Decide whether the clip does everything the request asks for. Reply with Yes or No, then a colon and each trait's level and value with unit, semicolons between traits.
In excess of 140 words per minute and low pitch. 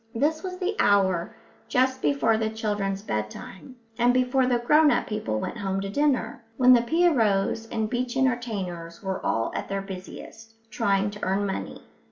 No: average, 170 wpm; high, 220 Hz